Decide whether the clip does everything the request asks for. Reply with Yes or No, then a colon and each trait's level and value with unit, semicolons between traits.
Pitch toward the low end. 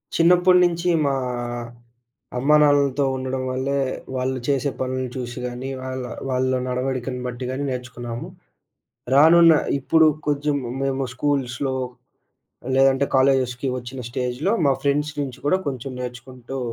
Yes: low, 130 Hz